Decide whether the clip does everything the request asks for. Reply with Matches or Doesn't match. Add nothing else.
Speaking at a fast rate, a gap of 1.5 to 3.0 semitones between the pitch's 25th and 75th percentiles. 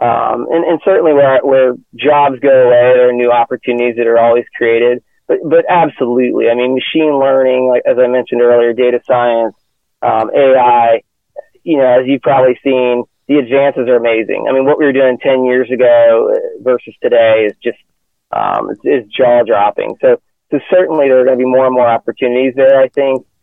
Doesn't match